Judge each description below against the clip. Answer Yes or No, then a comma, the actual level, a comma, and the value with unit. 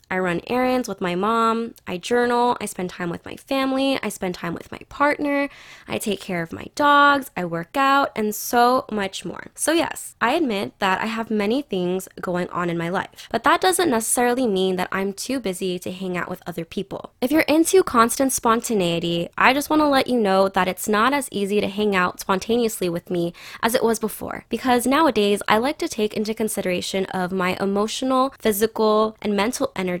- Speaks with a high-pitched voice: Yes, high, 215 Hz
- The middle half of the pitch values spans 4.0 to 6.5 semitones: Yes, average, 5.3 semitones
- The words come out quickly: Yes, fast, 210 wpm